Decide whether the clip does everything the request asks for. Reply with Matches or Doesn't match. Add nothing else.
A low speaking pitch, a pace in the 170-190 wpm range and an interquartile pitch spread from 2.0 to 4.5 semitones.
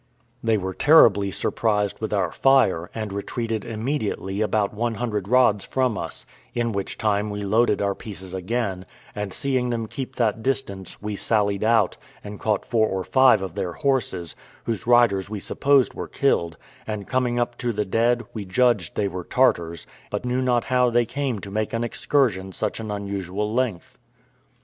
Matches